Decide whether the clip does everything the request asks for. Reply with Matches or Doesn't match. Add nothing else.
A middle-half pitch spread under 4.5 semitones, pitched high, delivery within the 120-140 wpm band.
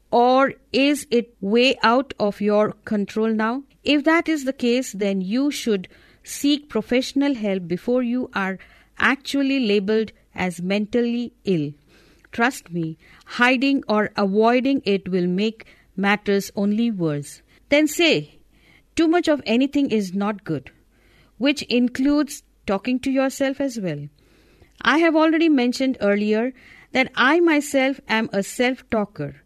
Doesn't match